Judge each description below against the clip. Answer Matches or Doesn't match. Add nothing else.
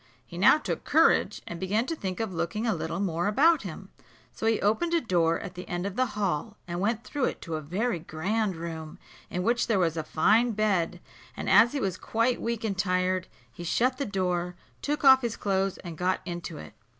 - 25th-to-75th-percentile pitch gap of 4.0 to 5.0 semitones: Matches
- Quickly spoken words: Matches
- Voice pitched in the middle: Doesn't match